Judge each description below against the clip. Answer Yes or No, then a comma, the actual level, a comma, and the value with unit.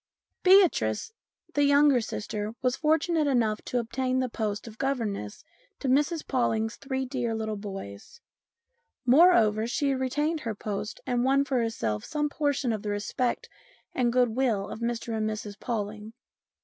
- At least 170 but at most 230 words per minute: No, average, 150 wpm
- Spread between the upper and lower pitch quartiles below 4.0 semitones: No, average, 4.3 semitones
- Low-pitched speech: No, high, 240 Hz